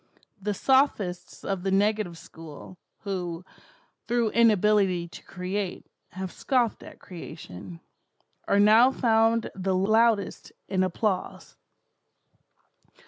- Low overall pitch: No, high, 195 Hz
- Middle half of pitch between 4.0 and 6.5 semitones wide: No, average, 3.5 semitones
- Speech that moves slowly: Yes, slow, 100 wpm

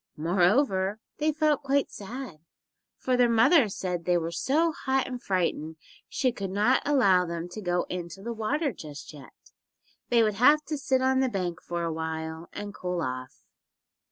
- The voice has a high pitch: Yes, high, 200 Hz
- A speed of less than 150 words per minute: No, average, 175 wpm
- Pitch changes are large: Yes, wide, 7.2 semitones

